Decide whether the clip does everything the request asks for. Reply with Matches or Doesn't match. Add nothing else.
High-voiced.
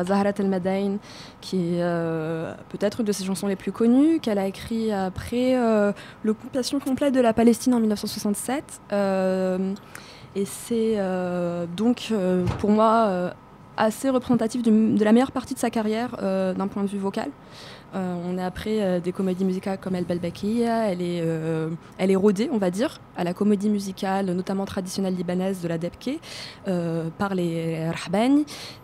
Matches